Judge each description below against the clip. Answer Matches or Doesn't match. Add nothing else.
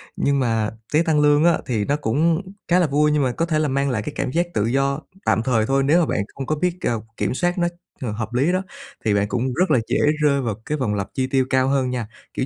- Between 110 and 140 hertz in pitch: Matches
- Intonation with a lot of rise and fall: Doesn't match